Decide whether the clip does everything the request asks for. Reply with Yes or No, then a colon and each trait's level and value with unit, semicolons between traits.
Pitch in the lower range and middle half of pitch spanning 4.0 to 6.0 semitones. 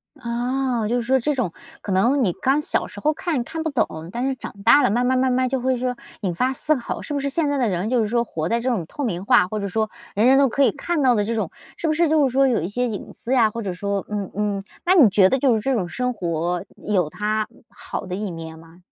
No: high, 235 Hz; average, 4.7 semitones